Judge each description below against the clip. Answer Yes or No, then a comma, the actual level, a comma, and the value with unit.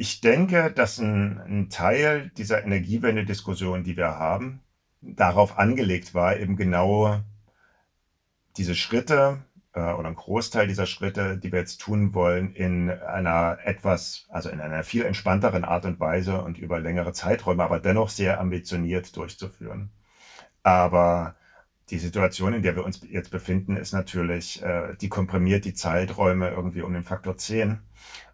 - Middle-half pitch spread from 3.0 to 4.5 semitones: No, narrow, 2.5 semitones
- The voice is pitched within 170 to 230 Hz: No, very low, 95 Hz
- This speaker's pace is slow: No, average, 150 wpm